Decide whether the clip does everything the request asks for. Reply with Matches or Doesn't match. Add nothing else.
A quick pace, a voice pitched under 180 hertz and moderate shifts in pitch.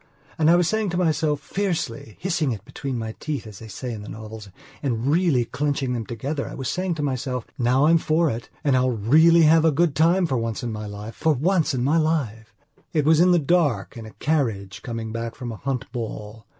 Doesn't match